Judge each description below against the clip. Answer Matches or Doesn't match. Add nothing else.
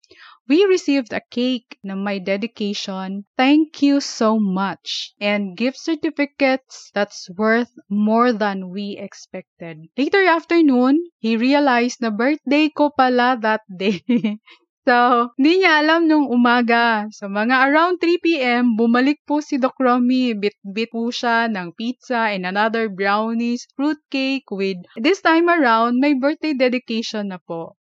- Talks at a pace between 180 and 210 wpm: Doesn't match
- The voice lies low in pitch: Doesn't match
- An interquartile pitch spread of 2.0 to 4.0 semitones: Doesn't match